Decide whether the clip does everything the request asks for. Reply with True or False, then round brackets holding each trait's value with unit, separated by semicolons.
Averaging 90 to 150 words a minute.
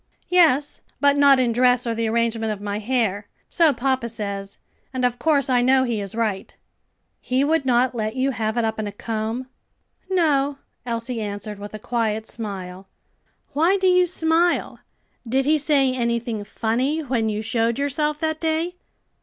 False (170 wpm)